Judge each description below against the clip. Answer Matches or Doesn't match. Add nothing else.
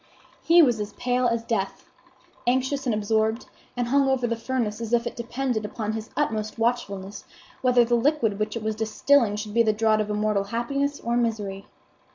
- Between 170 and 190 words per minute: Matches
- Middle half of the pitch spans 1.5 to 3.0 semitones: Matches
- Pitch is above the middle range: Matches